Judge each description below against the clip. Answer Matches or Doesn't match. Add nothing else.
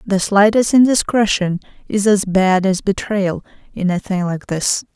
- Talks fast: Doesn't match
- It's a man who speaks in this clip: Doesn't match